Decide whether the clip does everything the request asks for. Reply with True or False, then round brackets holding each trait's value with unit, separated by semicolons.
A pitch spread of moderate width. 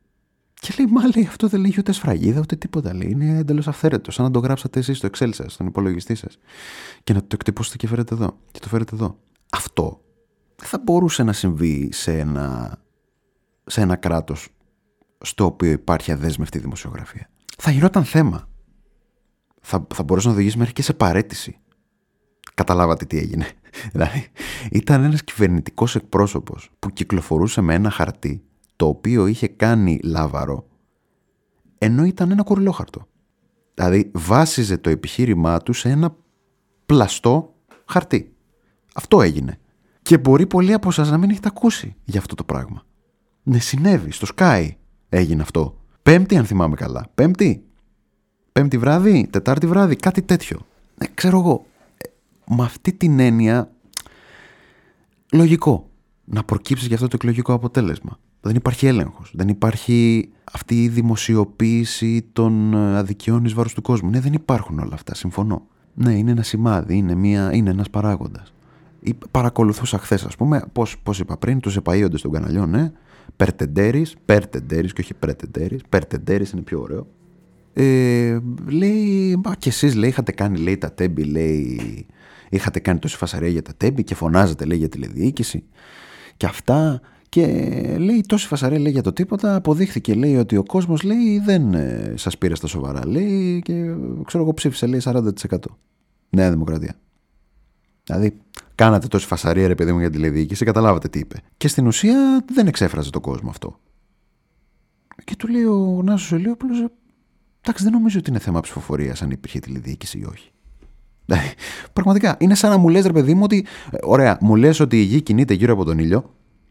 False (8.6 semitones)